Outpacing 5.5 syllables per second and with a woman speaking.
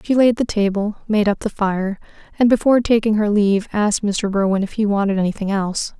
Yes: 6.0 syllables/s; female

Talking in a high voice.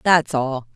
No: medium, 140 Hz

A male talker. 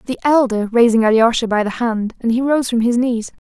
No: female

